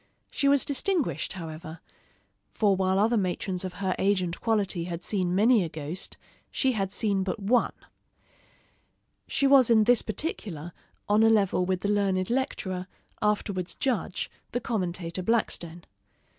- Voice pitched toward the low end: No, high, 195 Hz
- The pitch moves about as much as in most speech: Yes, average, 3.7 semitones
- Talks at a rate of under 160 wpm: Yes, average, 145 wpm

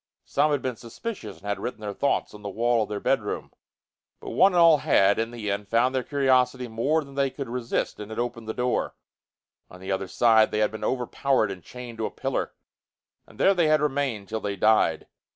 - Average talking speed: No, fast, 225 wpm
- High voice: No, low, 120 Hz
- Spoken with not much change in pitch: No, average, 4.1 semitones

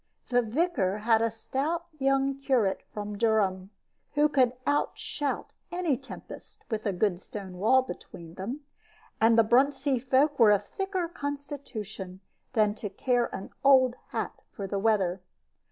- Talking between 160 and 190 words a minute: No, average, 145 wpm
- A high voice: Yes, high, 235 Hz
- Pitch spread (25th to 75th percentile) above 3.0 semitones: Yes, average, 5.1 semitones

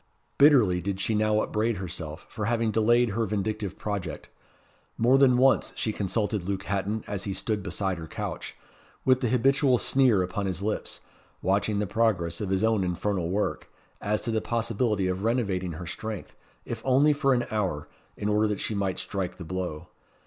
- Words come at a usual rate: Yes, average, 180 wpm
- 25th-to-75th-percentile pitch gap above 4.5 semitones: No, average, 3.4 semitones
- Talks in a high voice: No, low, 105 Hz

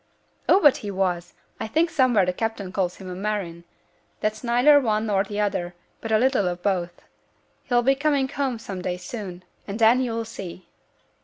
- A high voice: Yes, high, 215 Hz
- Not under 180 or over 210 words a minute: Yes, average, 185 wpm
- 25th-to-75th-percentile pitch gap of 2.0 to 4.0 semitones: No, average, 5.0 semitones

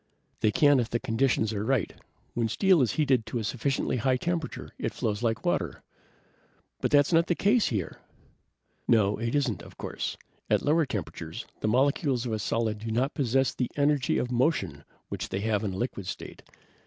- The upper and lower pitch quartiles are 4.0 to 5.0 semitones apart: Yes, average, 4.5 semitones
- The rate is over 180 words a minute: Yes, average, 190 wpm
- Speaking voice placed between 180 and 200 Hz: No, low, 120 Hz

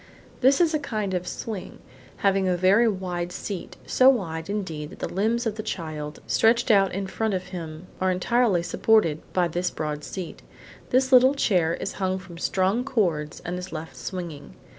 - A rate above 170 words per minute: Yes, average, 185 wpm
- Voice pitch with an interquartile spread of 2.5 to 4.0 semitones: No, average, 4.4 semitones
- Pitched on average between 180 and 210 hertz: Yes, high, 190 Hz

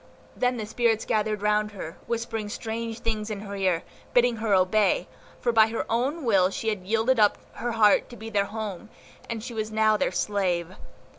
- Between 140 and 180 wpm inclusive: No, average, 195 wpm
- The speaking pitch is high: Yes, high, 215 Hz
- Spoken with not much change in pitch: Yes, narrow, 1.9 semitones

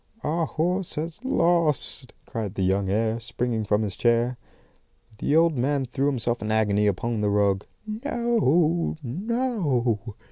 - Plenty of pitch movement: Yes, wide, 7.5 semitones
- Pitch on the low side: Yes, low, 125 Hz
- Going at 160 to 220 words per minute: No, average, 140 wpm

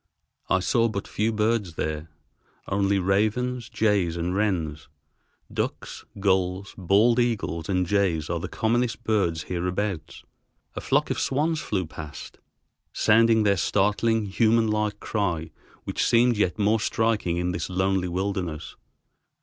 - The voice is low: Yes, low, 100 Hz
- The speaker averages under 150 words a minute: Yes, slow, 135 wpm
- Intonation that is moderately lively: Yes, average, 3.7 semitones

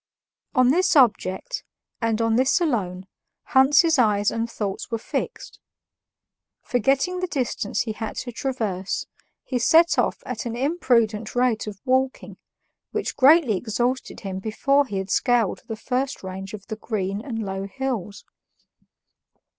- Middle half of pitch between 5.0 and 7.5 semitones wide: No, average, 4.2 semitones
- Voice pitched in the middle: No, high, 230 Hz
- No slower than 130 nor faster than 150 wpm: Yes, average, 140 wpm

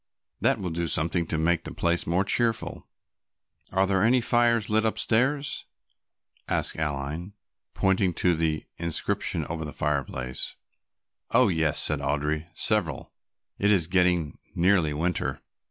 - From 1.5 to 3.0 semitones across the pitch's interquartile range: No, average, 4.1 semitones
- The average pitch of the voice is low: Yes, very low, 85 Hz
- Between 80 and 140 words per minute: Yes, slow, 135 wpm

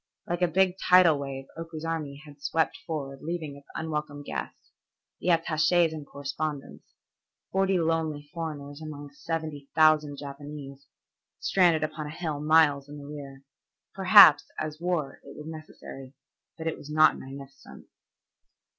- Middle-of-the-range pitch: Yes, medium, 155 Hz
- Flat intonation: Yes, narrow, 2.3 semitones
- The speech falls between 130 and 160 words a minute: Yes, average, 140 wpm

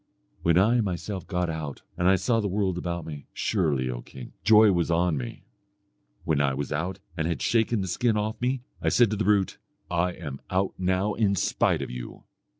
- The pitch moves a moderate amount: Yes, average, 4.5 semitones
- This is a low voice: Yes, very low, 90 Hz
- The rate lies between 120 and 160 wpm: No, fast, 205 wpm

